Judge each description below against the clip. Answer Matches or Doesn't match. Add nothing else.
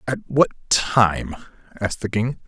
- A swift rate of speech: Doesn't match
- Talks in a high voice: Doesn't match